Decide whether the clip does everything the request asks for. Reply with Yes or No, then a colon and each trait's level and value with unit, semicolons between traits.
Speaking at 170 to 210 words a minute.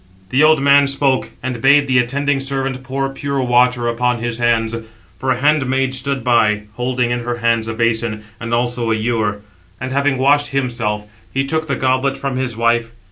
Yes: average, 190 wpm